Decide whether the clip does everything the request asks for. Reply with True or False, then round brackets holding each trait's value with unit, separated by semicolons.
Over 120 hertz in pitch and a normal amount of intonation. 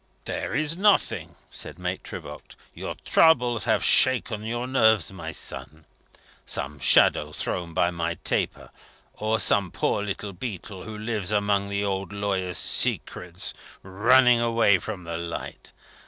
False (100 Hz; 4.4 semitones)